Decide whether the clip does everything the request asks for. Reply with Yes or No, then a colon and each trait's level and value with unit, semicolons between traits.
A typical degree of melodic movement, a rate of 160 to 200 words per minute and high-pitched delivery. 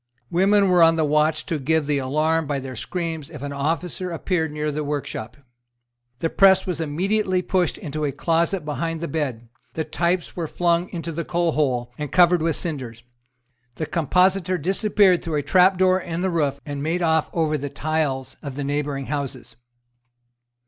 No: average, 3.4 semitones; average, 175 wpm; medium, 160 Hz